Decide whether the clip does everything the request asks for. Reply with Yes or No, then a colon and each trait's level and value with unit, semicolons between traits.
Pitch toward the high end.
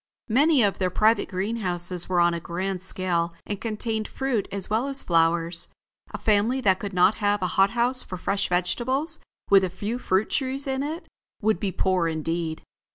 Yes: high, 200 Hz